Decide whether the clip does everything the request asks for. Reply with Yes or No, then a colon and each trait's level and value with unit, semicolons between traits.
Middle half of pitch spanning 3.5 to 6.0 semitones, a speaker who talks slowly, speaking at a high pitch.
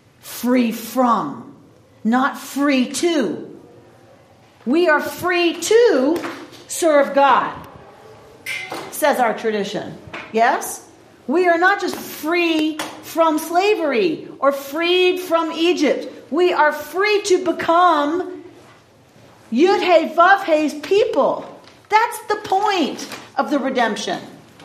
Yes: average, 4.1 semitones; slow, 95 wpm; very high, 325 Hz